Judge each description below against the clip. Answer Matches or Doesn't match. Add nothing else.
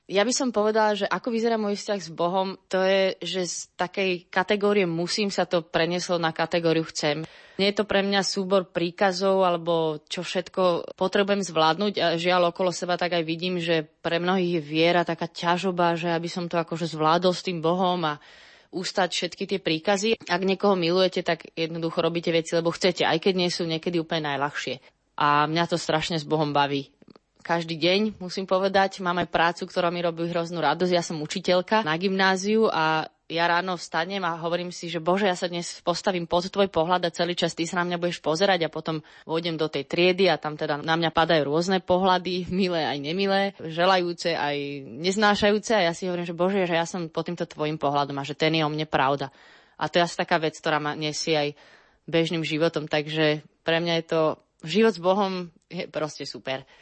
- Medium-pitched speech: Matches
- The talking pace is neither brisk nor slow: Doesn't match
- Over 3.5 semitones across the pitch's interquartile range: Doesn't match